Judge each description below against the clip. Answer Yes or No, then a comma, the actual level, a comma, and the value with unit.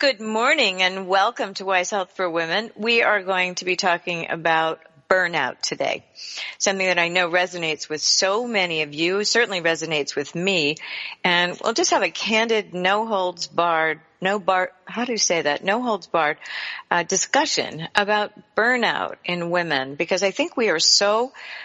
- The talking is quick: No, average, 175 wpm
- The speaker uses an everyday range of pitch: Yes, average, 3.5 semitones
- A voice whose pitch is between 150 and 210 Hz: Yes, medium, 185 Hz